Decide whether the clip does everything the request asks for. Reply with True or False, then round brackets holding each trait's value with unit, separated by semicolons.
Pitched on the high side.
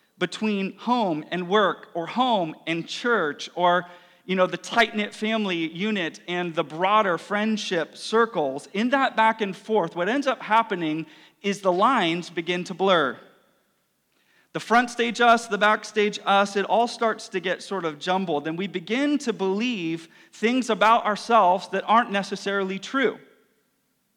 True (200 Hz)